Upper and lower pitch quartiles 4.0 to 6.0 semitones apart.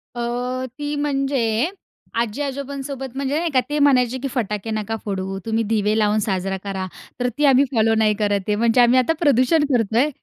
Yes: average, 4.3 semitones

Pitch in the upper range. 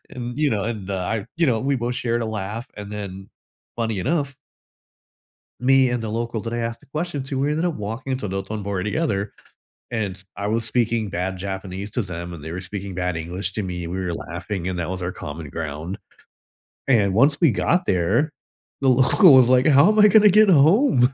No: low, 110 Hz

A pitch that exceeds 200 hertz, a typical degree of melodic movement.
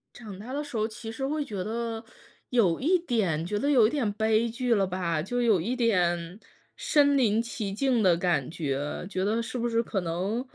Yes: high, 220 Hz; average, 4.8 semitones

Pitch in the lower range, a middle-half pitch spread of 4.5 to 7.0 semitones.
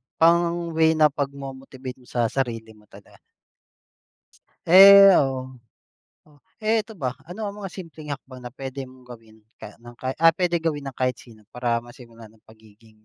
Yes: low, 130 Hz; wide, 5.4 semitones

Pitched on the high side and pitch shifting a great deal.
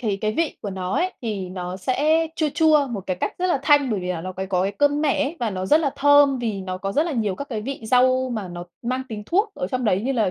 Yes: high, 245 Hz; wide, 6.8 semitones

